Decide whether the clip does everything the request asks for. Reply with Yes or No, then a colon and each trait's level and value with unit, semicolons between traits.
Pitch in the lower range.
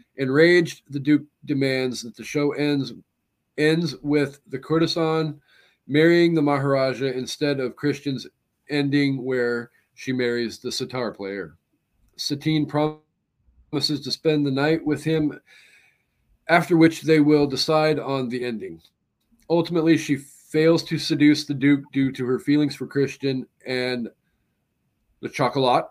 No: medium, 145 Hz